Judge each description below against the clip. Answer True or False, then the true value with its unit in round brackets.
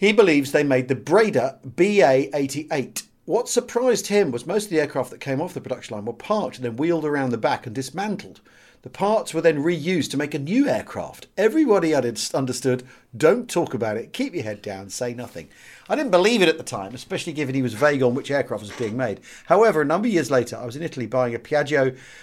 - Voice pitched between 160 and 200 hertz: False (140 Hz)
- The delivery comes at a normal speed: False (225 wpm)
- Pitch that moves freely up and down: True (5.8 semitones)